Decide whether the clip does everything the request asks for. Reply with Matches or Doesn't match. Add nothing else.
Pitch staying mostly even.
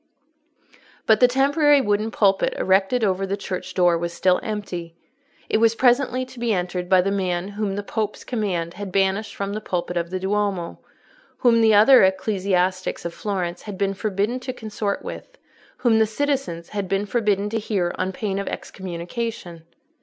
Doesn't match